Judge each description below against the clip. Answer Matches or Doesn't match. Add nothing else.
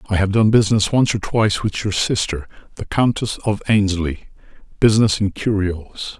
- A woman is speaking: Doesn't match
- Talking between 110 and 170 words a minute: Matches